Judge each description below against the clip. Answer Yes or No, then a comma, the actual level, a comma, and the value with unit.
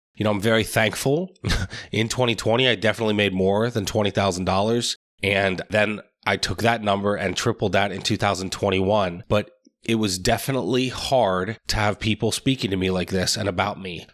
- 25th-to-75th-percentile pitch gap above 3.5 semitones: No, average, 2.8 semitones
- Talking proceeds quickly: No, average, 170 wpm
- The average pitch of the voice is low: Yes, low, 105 Hz